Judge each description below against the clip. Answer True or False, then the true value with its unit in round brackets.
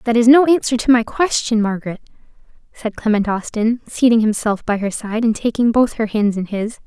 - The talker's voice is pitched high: True (225 Hz)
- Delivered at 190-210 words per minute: True (200 wpm)